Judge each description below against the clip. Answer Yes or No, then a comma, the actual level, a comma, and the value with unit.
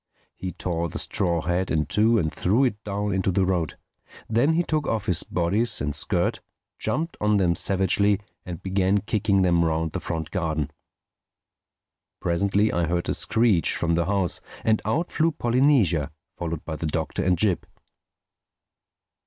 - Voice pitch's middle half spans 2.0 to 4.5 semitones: Yes, average, 3.9 semitones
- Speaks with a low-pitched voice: Yes, very low, 95 Hz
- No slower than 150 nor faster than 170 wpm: Yes, average, 160 wpm